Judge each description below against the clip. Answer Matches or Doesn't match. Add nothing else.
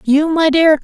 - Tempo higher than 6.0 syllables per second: Doesn't match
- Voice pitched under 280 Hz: Doesn't match